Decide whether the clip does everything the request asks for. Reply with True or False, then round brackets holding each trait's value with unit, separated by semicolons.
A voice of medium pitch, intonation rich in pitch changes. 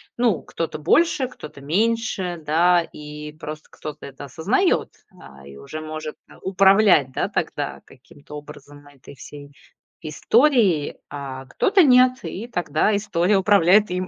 True (165 Hz; 6.0 semitones)